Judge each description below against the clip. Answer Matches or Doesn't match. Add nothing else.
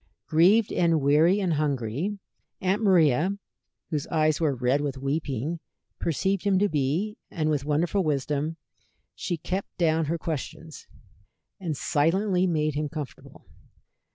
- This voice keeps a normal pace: Doesn't match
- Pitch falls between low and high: Matches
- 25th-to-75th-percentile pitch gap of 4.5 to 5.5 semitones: Doesn't match